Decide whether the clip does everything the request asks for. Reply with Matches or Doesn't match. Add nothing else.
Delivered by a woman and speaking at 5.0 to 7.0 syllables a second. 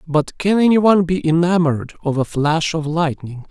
Doesn't match